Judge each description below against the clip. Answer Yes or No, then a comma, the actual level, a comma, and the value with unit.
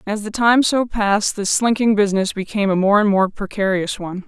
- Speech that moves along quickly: Yes, fast, 210 wpm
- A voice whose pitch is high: Yes, high, 205 Hz